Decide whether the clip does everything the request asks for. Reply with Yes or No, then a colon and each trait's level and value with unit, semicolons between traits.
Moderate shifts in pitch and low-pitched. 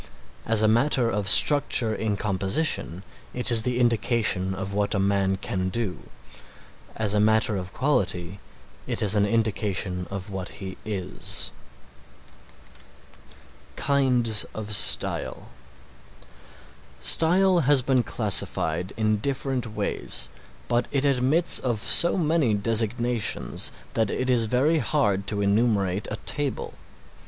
Yes: average, 4.1 semitones; low, 110 Hz